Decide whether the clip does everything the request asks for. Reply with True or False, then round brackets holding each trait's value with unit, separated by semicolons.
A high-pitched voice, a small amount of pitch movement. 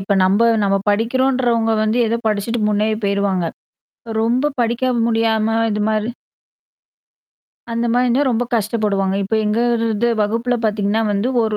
True (225 Hz; 2.3 semitones)